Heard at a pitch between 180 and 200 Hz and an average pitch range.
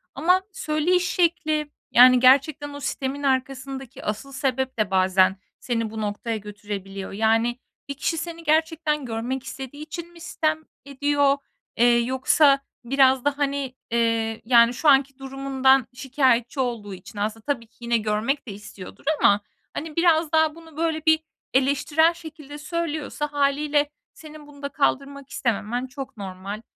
No: very high, 270 Hz; average, 4.3 semitones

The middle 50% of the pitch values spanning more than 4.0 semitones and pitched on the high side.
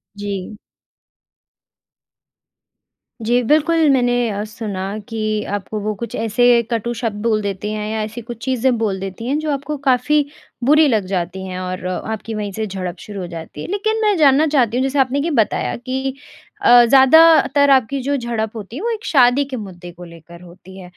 Yes: average, 5.1 semitones; high, 230 Hz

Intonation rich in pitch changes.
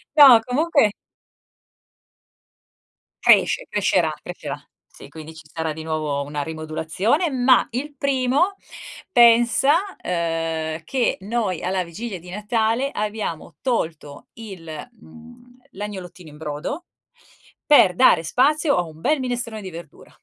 Yes: wide, 7.4 semitones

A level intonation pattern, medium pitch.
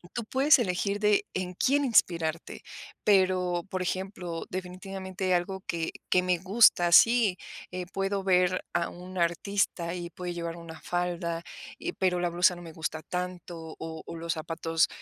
Yes: narrow, 2.0 semitones; medium, 180 Hz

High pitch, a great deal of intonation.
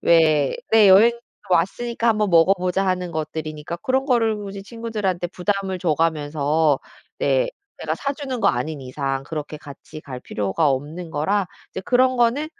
No: medium, 180 Hz; wide, 6.3 semitones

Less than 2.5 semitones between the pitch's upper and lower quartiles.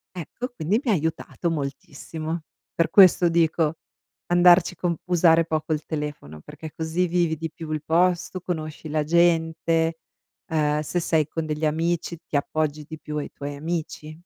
Yes: narrow, 2.0 semitones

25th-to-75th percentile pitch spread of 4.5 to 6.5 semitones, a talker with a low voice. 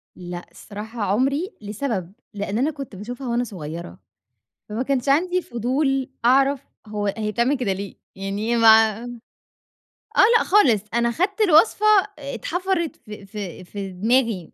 No: average, 5.3 semitones; high, 235 Hz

